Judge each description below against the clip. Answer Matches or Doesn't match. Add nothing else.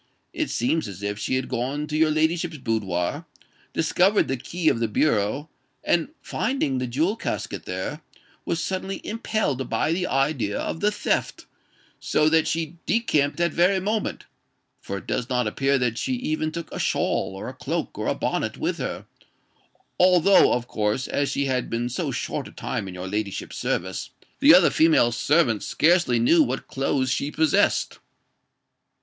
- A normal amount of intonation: Doesn't match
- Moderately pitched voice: Matches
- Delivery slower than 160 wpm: Doesn't match